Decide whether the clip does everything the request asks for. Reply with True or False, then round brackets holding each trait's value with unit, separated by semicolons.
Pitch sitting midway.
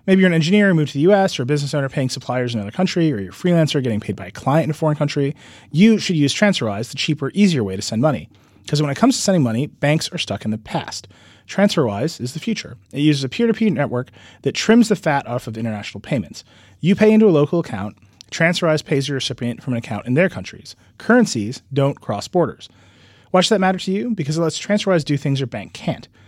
True (145 Hz)